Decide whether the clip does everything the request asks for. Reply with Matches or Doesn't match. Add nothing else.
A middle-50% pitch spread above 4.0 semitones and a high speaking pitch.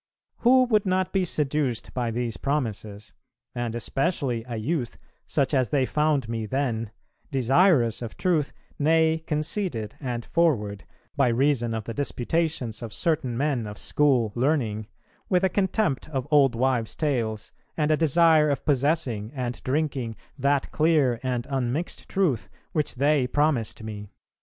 Doesn't match